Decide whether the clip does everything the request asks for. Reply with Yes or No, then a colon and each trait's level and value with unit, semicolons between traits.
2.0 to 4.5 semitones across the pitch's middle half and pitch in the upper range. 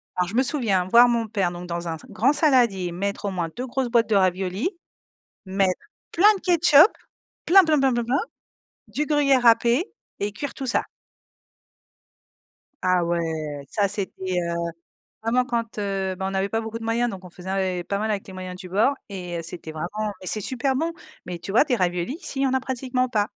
No: wide, 5.5 semitones; high, 210 Hz